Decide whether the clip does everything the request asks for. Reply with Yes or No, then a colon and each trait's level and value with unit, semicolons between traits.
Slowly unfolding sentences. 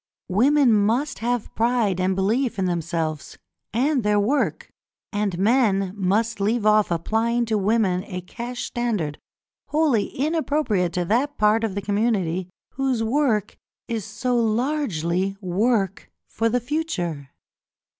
Yes: slow, 130 wpm